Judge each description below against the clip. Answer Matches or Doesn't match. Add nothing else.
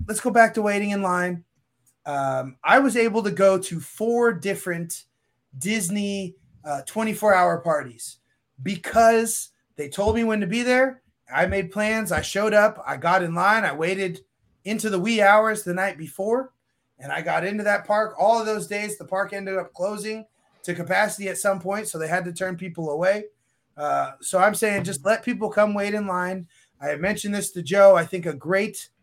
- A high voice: Matches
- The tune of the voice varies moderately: Matches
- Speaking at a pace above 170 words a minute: Matches